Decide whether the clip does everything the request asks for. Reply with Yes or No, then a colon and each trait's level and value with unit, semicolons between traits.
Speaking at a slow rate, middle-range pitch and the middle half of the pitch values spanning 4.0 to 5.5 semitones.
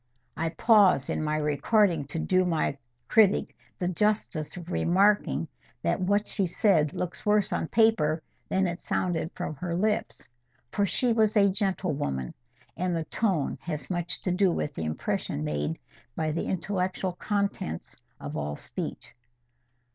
No: average, 150 wpm; medium, 180 Hz; average, 4.6 semitones